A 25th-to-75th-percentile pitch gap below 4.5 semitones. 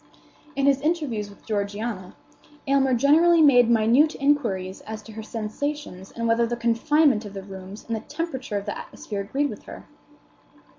No: average, 5.2 semitones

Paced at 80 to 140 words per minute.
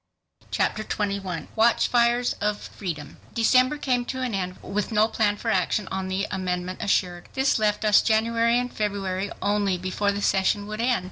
No: average, 165 wpm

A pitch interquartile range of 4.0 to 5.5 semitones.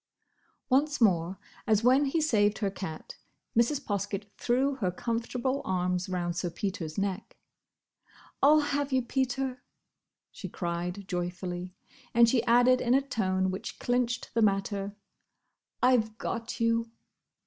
Yes: average, 5.2 semitones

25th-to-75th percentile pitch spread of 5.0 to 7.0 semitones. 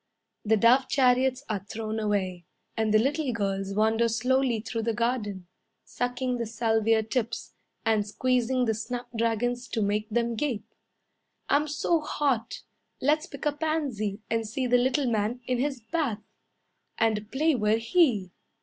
No: average, 3.1 semitones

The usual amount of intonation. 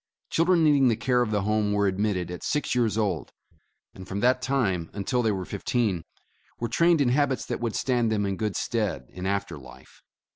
Yes: average, 4.4 semitones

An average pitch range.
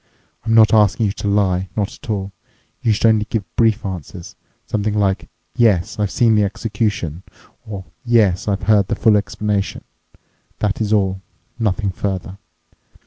No: narrow, 2.1 semitones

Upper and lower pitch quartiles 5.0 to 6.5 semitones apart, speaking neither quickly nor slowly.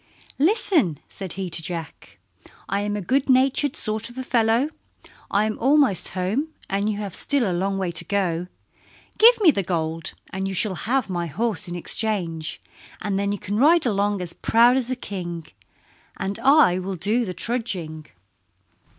Yes: wide, 5.4 semitones; average, 175 wpm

